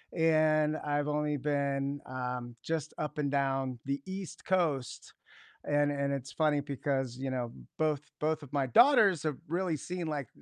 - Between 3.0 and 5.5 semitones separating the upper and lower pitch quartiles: No, narrow, 2.4 semitones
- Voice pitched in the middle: Yes, medium, 145 Hz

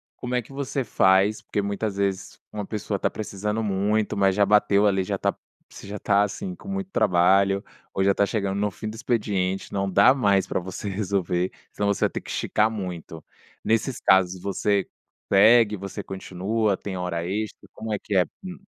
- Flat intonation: Yes, narrow, 2.0 semitones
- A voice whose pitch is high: No, low, 100 Hz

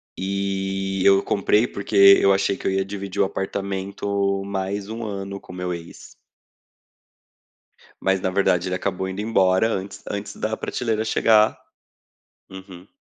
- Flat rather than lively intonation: Yes, narrow, 1.0 semitones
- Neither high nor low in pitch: No, very low, 95 Hz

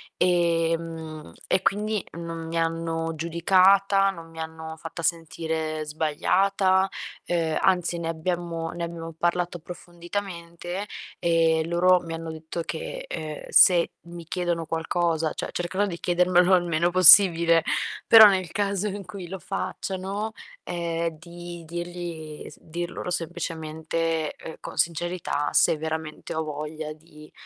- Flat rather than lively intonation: Yes, narrow, 1.7 semitones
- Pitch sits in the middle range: Yes, medium, 170 Hz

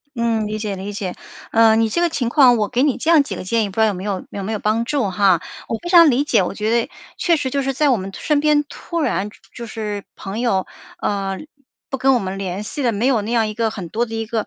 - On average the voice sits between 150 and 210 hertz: No, high, 225 Hz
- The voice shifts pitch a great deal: No, average, 4.2 semitones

